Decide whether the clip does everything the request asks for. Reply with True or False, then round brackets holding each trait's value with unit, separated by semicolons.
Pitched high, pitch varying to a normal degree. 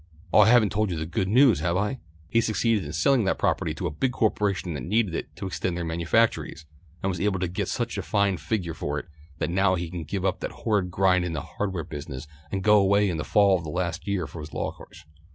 False (95 Hz; 3.8 semitones)